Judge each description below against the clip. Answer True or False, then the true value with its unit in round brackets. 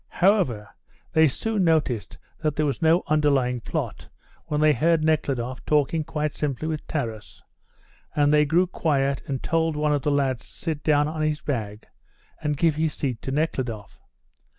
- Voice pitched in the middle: True (150 Hz)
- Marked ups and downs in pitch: False (2.8 semitones)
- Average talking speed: True (170 wpm)